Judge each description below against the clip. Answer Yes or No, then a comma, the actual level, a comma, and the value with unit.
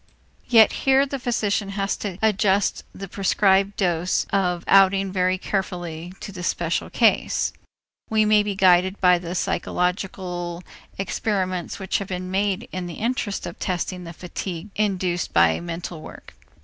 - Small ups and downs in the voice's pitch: Yes, narrow, 2.2 semitones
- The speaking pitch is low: No, high, 190 Hz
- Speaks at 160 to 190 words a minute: No, average, 150 wpm